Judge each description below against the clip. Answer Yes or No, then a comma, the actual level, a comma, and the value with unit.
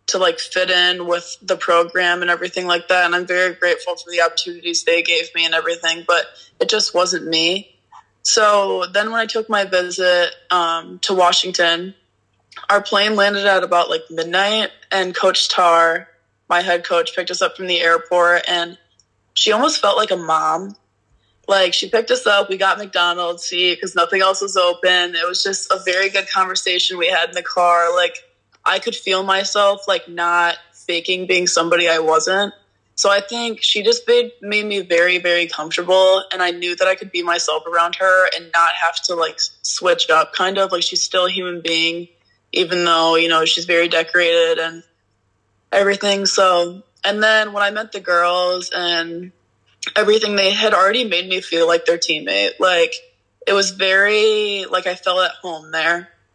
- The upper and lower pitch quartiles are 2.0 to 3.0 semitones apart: Yes, narrow, 2.5 semitones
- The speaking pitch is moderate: Yes, medium, 180 Hz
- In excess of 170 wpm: Yes, average, 185 wpm